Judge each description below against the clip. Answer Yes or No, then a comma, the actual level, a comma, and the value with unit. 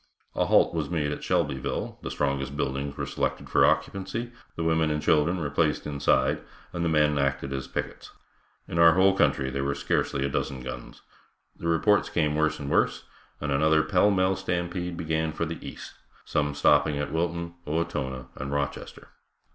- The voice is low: Yes, very low, 75 Hz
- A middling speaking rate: Yes, average, 180 wpm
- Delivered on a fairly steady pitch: No, average, 3.3 semitones